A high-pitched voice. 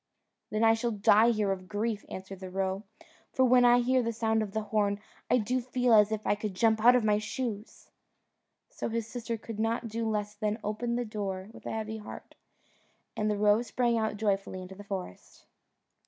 Yes: high, 215 Hz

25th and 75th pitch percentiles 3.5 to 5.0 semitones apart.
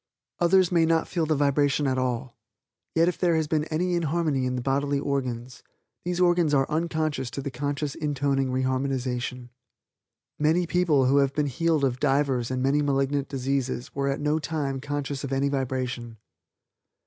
No: average, 2.9 semitones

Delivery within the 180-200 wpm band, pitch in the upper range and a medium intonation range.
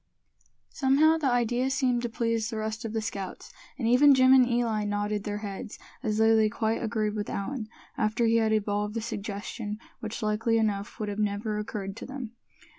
No: average, 190 wpm; high, 220 Hz; narrow, 2.3 semitones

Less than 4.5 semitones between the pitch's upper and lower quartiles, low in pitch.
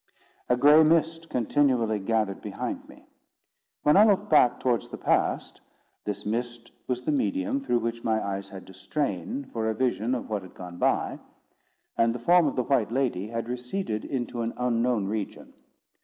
No: average, 4.9 semitones; low, 120 Hz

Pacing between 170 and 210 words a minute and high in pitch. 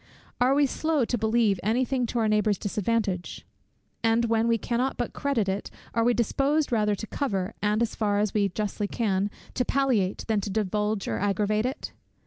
Yes: average, 190 wpm; high, 220 Hz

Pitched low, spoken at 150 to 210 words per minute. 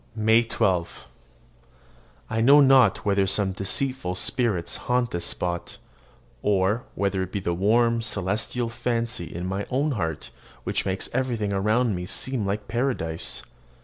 No: low, 105 Hz; average, 140 wpm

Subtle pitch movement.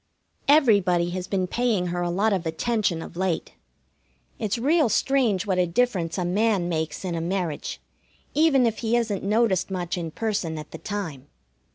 No: average, 4.5 semitones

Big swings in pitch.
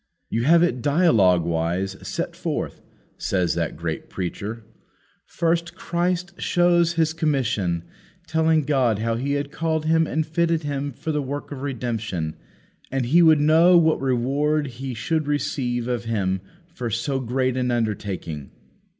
Yes: wide, 5.8 semitones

